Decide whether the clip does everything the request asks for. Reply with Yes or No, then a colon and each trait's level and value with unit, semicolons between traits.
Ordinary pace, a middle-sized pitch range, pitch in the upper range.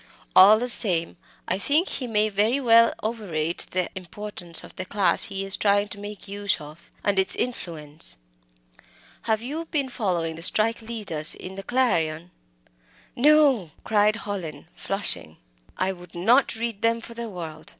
Yes: average, 160 wpm; average, 4.7 semitones; high, 205 Hz